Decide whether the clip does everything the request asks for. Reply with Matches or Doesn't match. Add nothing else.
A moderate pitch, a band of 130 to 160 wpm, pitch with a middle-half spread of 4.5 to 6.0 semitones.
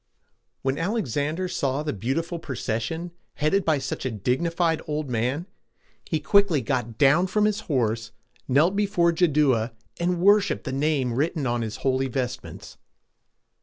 Matches